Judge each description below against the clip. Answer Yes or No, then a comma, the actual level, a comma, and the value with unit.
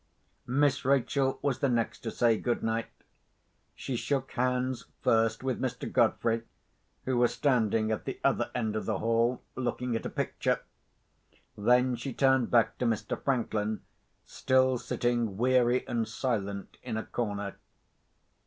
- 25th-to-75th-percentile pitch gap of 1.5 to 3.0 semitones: Yes, narrow, 2.4 semitones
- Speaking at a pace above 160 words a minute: No, average, 145 wpm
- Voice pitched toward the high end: No, low, 120 Hz